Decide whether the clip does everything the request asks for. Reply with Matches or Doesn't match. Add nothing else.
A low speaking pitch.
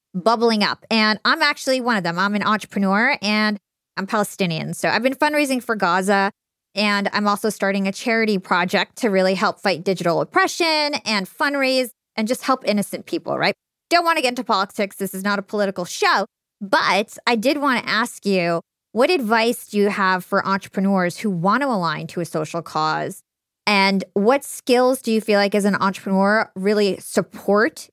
Doesn't match